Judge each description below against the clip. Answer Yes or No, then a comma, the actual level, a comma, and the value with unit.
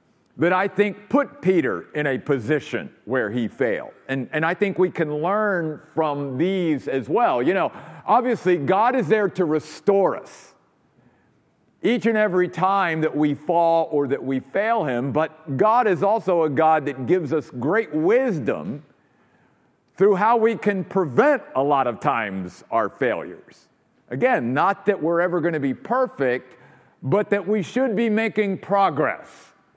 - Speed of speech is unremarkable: Yes, average, 165 wpm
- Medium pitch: Yes, medium, 180 Hz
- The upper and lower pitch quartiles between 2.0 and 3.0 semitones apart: No, average, 5.1 semitones